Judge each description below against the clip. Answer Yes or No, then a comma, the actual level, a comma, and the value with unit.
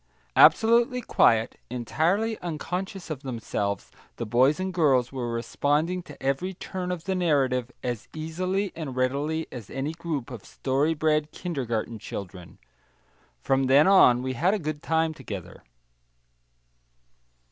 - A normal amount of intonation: No, wide, 5.7 semitones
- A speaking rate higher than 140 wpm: No, slow, 135 wpm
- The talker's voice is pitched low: No, medium, 145 Hz